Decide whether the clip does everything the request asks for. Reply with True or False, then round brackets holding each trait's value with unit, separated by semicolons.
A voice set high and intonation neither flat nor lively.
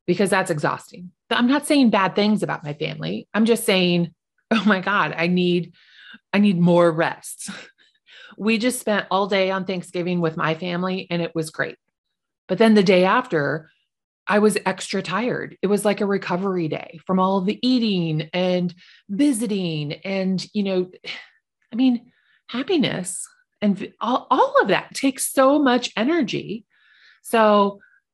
True (195 Hz; 4.0 semitones)